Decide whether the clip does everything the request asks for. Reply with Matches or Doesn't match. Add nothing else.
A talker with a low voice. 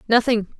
Doesn't match